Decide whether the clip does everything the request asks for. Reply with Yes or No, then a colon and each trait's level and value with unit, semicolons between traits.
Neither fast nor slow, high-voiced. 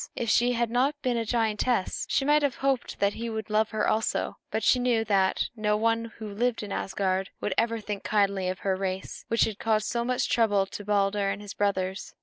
No: fast, 220 wpm; high, 215 Hz